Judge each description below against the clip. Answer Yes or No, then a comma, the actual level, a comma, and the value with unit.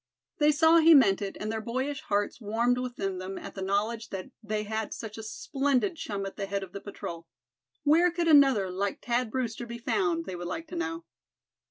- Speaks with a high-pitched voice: Yes, high, 230 Hz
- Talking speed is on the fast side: Yes, fast, 210 wpm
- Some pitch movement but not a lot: No, wide, 6.2 semitones